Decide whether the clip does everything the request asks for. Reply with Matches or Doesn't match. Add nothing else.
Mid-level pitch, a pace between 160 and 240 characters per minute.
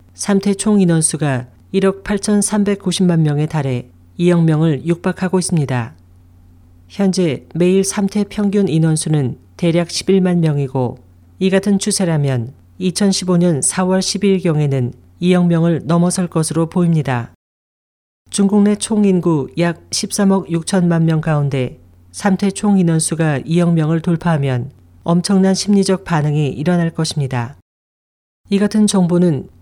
Matches